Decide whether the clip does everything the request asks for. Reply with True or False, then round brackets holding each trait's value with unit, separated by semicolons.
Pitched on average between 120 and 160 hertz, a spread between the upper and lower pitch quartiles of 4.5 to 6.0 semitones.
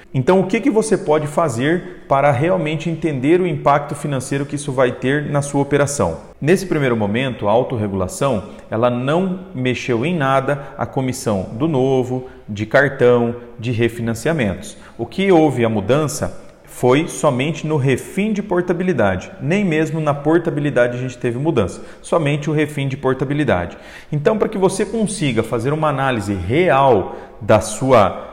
True (140 Hz; 4.9 semitones)